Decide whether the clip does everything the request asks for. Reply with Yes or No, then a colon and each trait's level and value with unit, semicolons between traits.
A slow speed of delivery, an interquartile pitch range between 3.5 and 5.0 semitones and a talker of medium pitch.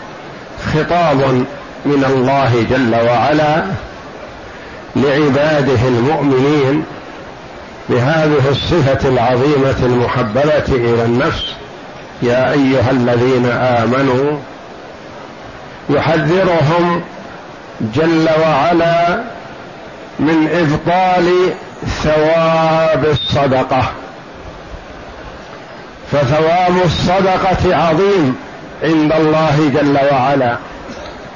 Yes: slow, 60 wpm; average, 3.8 semitones; medium, 145 Hz